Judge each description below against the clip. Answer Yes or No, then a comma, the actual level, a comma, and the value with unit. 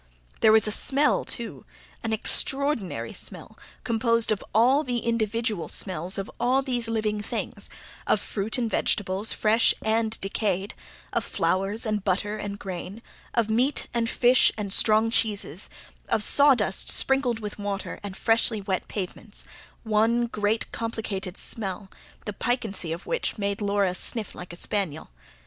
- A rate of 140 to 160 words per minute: Yes, average, 145 wpm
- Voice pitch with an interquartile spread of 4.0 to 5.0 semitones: No, narrow, 2.6 semitones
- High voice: Yes, high, 215 Hz